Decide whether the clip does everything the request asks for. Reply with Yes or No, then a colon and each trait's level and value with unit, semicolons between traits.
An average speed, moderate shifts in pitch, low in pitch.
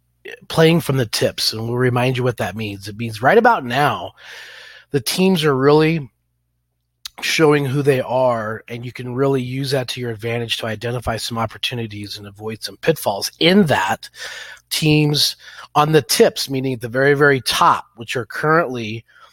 Yes: average, 175 wpm; average, 4.3 semitones; low, 125 Hz